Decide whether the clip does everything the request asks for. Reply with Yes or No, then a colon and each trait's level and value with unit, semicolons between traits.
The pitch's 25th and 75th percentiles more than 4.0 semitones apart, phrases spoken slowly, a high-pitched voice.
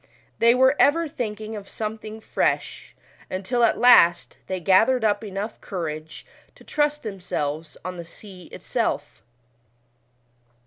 Yes: average, 4.5 semitones; slow, 125 wpm; high, 210 Hz